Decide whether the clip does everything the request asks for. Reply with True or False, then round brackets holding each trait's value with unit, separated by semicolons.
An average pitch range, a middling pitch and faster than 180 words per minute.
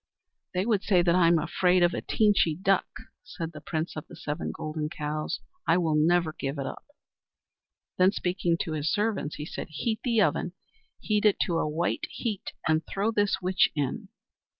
True (4.1 semitones; 175 Hz; 190 wpm)